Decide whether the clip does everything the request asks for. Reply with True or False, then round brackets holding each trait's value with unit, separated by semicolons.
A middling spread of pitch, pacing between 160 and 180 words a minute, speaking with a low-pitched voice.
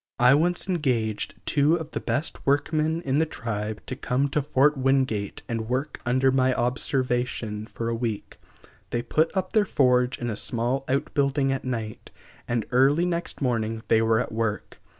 True (3.6 semitones; 170 wpm; 130 Hz)